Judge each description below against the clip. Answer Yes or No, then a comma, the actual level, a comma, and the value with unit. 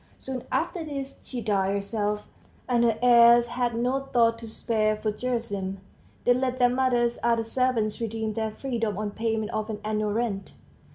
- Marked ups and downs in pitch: No, narrow, 2.4 semitones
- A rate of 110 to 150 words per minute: No, average, 170 wpm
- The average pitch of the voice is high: Yes, high, 230 Hz